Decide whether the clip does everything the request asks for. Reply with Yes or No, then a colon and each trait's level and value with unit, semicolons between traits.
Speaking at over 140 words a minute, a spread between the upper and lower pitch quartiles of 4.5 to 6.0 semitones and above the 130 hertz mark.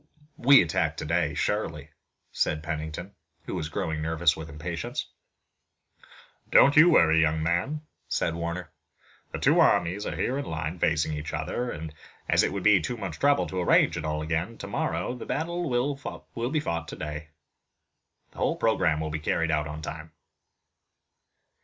No: average, 160 wpm; wide, 5.6 semitones; very low, 80 Hz